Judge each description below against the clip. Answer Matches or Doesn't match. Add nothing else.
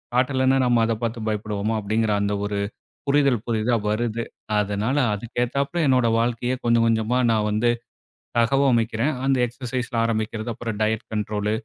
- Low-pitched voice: Matches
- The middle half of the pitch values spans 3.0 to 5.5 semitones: Doesn't match